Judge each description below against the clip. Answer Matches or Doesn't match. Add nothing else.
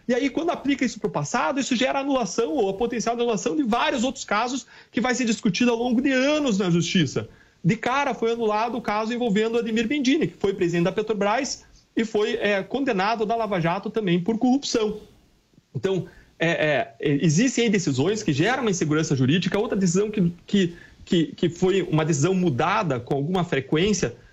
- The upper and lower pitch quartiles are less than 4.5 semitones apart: Doesn't match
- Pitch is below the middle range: Doesn't match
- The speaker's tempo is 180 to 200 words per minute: Matches